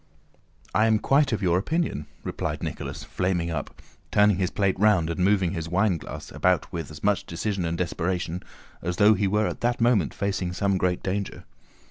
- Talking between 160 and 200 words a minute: Yes, average, 180 wpm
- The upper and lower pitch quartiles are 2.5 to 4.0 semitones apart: Yes, average, 3.0 semitones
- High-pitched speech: No, very low, 95 Hz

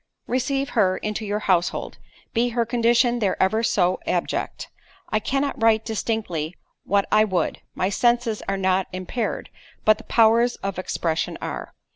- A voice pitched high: Yes, high, 215 Hz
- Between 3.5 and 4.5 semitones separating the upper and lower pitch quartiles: Yes, average, 3.8 semitones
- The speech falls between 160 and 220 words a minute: No, average, 145 wpm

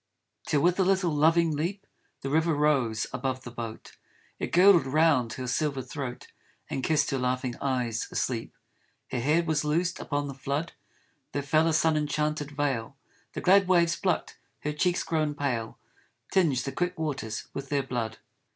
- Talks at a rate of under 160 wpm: No, average, 170 wpm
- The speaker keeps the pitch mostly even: No, average, 3.8 semitones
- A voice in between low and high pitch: Yes, medium, 145 Hz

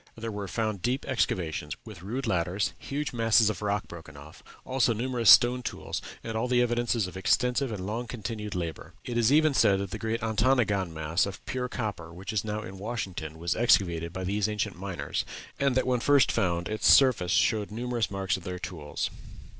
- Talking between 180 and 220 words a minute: Yes, average, 195 wpm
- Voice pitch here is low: Yes, low, 105 Hz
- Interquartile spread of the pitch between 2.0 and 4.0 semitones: No, average, 4.6 semitones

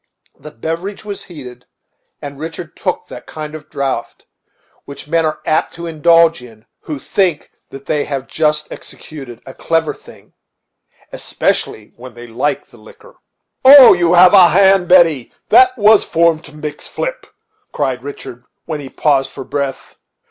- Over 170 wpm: No, average, 155 wpm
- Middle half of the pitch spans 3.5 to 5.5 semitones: Yes, average, 4.0 semitones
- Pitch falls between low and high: Yes, medium, 155 Hz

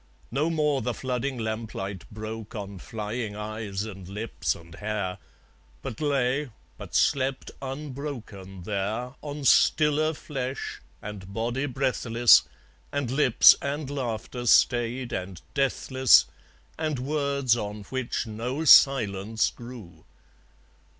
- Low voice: Yes, low, 120 Hz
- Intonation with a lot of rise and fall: No, average, 4.4 semitones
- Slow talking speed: Yes, slow, 110 wpm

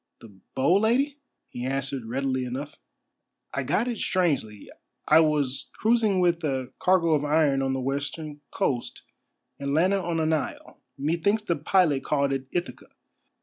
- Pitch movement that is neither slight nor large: Yes, average, 4.6 semitones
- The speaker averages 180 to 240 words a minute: No, average, 150 wpm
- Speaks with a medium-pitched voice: Yes, medium, 150 Hz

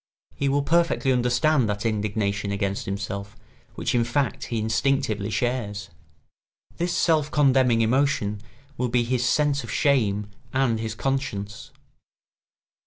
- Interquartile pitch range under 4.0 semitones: No, average, 4.8 semitones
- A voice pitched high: No, low, 120 Hz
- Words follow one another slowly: Yes, slow, 125 wpm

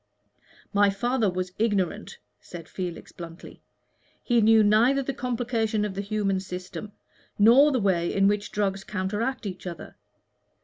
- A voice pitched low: No, high, 205 Hz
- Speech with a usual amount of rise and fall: Yes, average, 3.3 semitones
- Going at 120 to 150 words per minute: Yes, average, 140 wpm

